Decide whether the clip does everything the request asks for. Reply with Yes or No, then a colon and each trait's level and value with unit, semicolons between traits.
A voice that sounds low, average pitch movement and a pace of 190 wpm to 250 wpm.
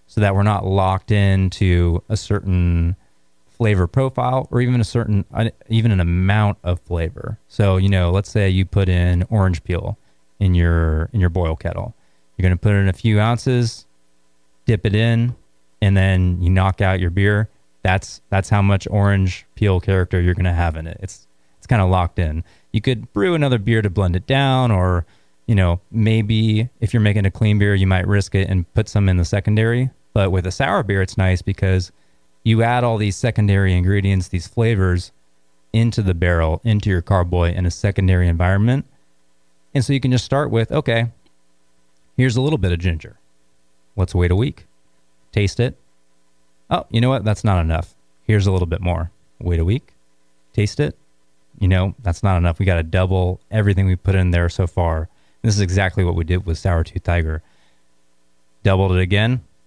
Yes: very low, 95 Hz; average, 3.8 semitones; average, 195 wpm